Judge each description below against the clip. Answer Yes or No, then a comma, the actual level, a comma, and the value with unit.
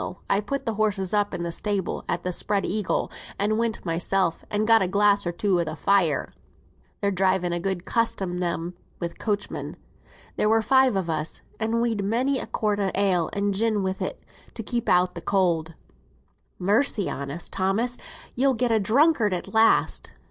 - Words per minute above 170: Yes, average, 185 wpm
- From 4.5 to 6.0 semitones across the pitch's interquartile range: No, average, 3.6 semitones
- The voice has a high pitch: Yes, high, 200 Hz